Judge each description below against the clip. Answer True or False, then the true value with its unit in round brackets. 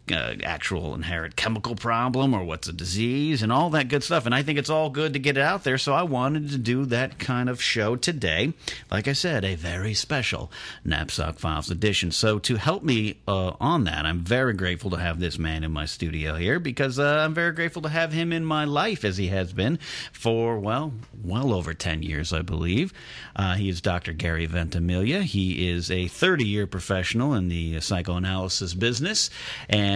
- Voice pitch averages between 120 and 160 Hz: False (105 Hz)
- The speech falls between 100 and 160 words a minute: False (205 wpm)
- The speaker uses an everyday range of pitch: False (7.6 semitones)